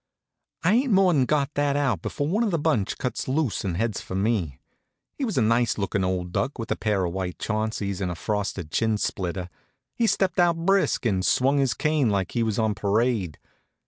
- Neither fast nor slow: No, fast, 210 wpm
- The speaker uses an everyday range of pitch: No, wide, 6.8 semitones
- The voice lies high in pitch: No, low, 115 Hz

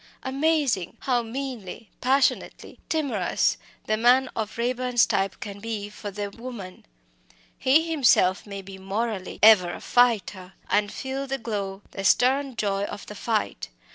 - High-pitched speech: Yes, high, 225 Hz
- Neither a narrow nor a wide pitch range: Yes, average, 4.4 semitones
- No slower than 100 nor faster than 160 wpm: Yes, average, 140 wpm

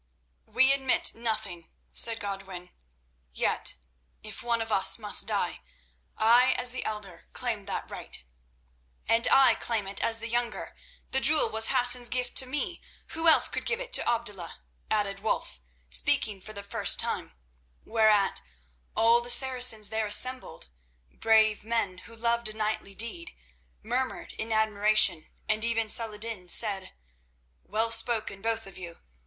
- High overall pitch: Yes, high, 225 Hz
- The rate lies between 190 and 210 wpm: No, average, 150 wpm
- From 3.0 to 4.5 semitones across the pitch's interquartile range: No, narrow, 2.5 semitones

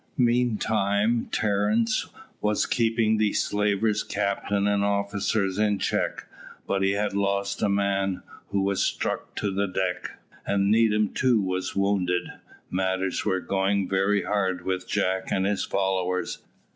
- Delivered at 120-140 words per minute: Yes, slow, 135 wpm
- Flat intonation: Yes, narrow, 1.5 semitones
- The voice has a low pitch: Yes, low, 100 Hz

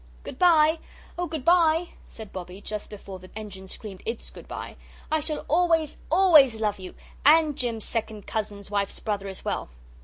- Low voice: No, high, 225 Hz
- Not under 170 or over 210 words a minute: Yes, average, 175 wpm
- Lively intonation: Yes, wide, 7.7 semitones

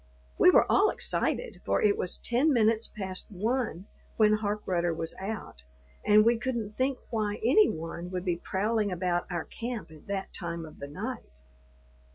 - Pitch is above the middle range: Yes, high, 205 Hz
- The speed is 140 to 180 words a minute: Yes, average, 170 wpm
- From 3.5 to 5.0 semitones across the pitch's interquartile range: Yes, average, 4.5 semitones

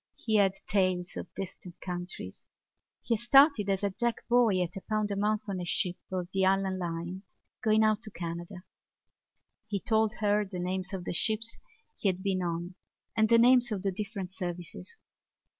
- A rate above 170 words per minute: Yes, average, 185 wpm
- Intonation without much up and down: No, average, 3.1 semitones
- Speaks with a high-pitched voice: Yes, high, 195 Hz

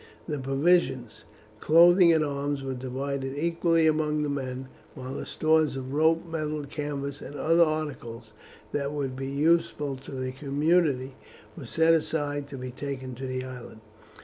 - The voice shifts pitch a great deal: No, average, 3.0 semitones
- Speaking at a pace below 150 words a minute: No, average, 155 wpm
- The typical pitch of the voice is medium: Yes, medium, 145 Hz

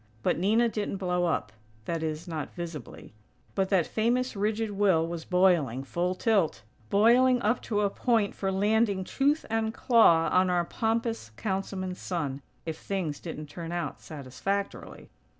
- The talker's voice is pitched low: No, high, 190 Hz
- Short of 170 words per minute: Yes, average, 150 wpm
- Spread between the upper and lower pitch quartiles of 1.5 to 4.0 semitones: No, average, 4.7 semitones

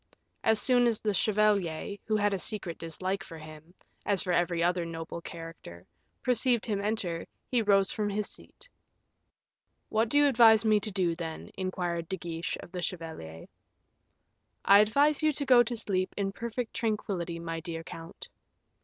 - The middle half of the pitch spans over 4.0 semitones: Yes, average, 4.5 semitones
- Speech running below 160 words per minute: No, average, 170 wpm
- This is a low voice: No, high, 195 Hz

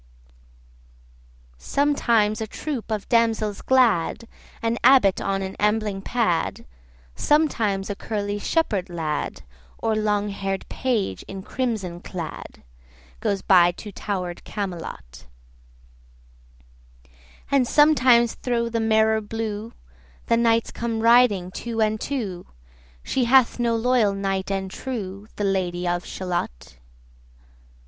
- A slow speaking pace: Yes, slow, 120 wpm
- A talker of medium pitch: No, high, 215 Hz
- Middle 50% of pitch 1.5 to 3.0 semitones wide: No, average, 3.4 semitones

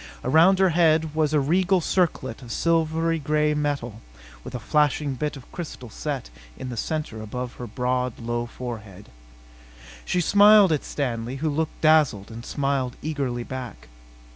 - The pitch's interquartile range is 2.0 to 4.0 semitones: No, average, 4.5 semitones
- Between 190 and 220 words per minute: No, average, 155 wpm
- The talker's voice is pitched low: No, medium, 145 Hz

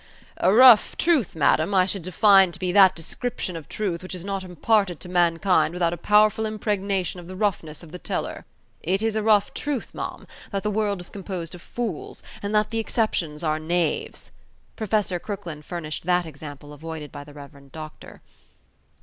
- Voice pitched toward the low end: No, medium, 185 Hz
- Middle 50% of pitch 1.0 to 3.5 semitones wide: No, average, 4.2 semitones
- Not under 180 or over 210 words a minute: Yes, average, 185 wpm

